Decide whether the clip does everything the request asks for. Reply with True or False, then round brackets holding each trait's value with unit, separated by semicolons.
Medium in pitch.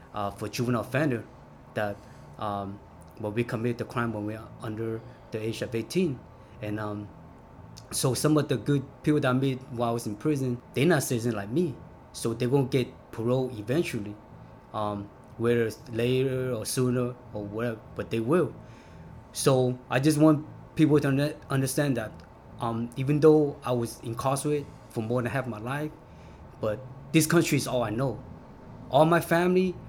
False (125 Hz)